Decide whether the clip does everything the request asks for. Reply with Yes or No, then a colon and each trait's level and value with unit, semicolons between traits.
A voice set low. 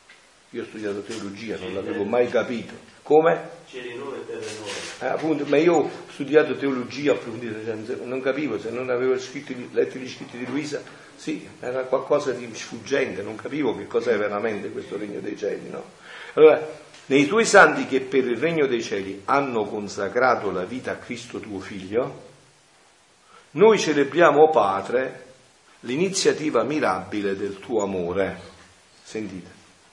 Yes: low, 130 Hz